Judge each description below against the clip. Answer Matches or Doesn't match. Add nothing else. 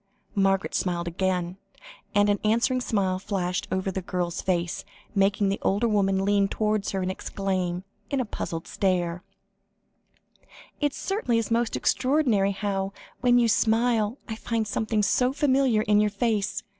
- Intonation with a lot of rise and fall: Doesn't match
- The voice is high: Matches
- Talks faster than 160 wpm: Doesn't match